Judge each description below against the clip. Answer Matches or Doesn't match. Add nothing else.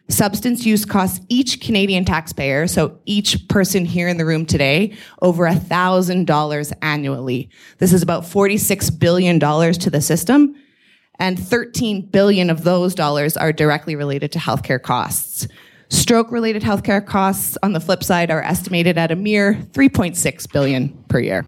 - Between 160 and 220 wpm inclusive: Doesn't match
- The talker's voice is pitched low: Doesn't match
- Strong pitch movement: Doesn't match